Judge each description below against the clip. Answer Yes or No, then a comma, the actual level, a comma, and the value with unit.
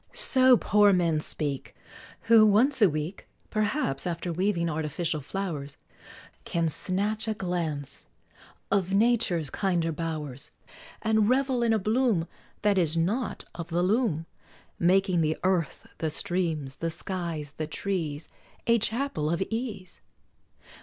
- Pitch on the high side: No, medium, 180 Hz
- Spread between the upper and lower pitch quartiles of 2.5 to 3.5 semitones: No, average, 5.0 semitones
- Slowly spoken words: Yes, slow, 130 wpm